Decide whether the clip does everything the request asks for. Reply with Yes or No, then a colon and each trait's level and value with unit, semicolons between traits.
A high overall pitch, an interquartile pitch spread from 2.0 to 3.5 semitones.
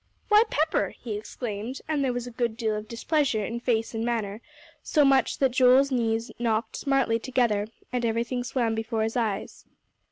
Yes: high, 235 Hz; narrow, 2.6 semitones